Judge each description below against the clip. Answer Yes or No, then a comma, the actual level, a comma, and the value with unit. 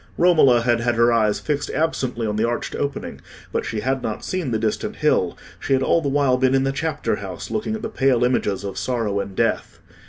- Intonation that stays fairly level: No, average, 3.8 semitones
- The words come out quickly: Yes, fast, 225 wpm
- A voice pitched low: Yes, low, 125 Hz